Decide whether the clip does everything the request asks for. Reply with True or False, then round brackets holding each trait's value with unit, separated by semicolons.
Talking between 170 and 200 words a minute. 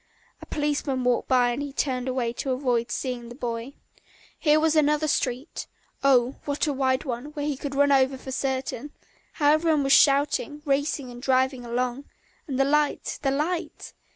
True (180 wpm)